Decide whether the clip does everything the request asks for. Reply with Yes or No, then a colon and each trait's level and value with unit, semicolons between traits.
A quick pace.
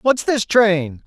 No: average, 170 wpm